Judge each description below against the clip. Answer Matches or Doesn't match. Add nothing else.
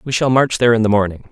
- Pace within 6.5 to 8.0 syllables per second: Matches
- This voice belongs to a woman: Doesn't match